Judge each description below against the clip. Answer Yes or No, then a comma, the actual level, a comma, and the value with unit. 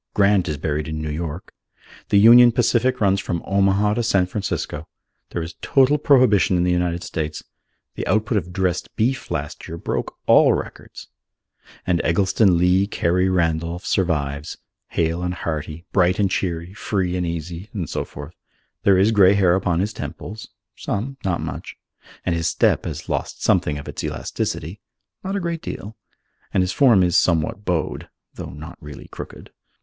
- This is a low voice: Yes, very low, 90 Hz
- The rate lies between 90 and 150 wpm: No, average, 170 wpm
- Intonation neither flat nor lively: Yes, average, 3.6 semitones